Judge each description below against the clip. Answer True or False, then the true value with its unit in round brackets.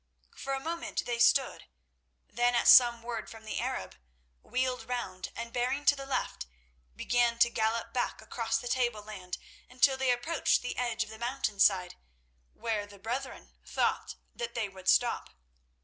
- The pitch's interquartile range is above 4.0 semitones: False (2.4 semitones)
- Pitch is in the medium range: False (235 Hz)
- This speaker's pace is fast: False (160 wpm)